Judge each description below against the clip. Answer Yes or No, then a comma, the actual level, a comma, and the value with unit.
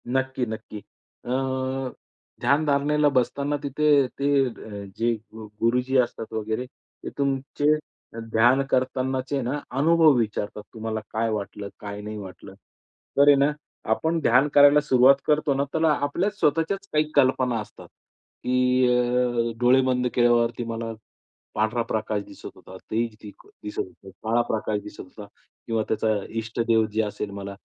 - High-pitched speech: No, low, 125 Hz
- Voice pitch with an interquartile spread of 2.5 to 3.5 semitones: No, average, 3.9 semitones